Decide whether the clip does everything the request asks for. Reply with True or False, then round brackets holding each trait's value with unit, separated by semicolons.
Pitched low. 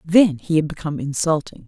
False (160 Hz)